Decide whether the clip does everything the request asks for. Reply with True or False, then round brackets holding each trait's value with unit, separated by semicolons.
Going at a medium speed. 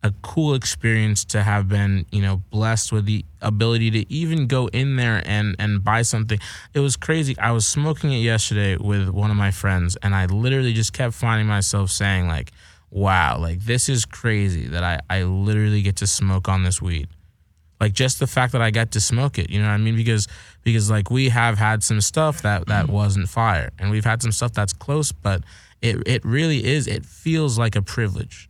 False (215 wpm)